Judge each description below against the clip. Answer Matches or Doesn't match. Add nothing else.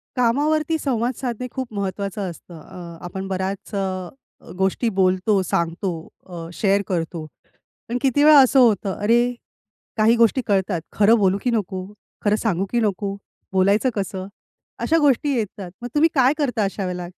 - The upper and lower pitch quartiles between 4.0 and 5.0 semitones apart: Matches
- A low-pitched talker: Doesn't match